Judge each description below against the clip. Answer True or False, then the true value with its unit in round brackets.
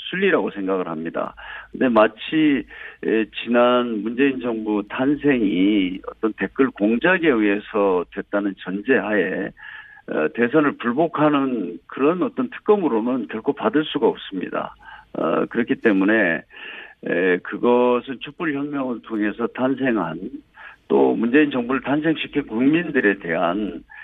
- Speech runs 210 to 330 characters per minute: True (260 characters per minute)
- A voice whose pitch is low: True (125 Hz)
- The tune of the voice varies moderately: False (5.9 semitones)